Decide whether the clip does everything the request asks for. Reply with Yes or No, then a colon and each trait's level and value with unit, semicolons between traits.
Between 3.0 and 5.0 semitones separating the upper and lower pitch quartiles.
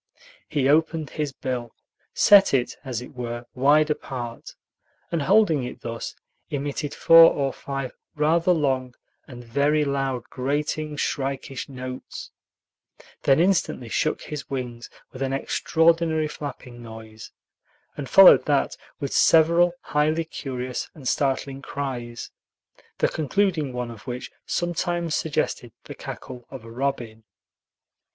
Yes: average, 3.7 semitones